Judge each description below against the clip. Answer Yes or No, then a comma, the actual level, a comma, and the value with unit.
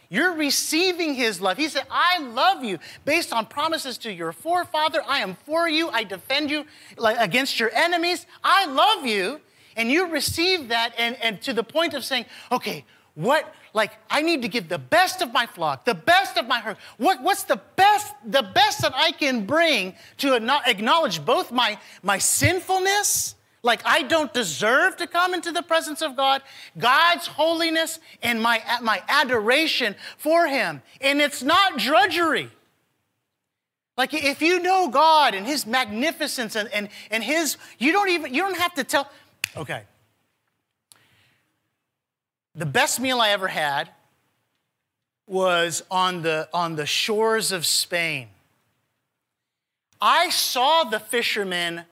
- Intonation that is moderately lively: No, wide, 6.9 semitones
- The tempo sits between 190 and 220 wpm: No, average, 155 wpm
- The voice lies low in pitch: No, very high, 275 Hz